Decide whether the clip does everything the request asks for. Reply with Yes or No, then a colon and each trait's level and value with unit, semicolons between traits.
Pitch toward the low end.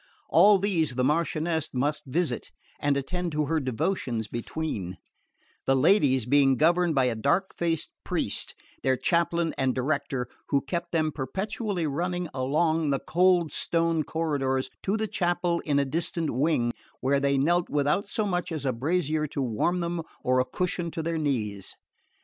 No: medium, 155 Hz